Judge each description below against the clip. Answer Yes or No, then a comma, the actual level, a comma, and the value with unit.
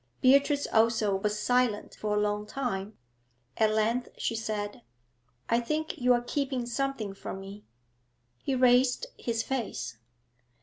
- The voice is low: No, high, 230 Hz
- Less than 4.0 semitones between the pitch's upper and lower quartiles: Yes, average, 3.5 semitones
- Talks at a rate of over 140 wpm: No, slow, 135 wpm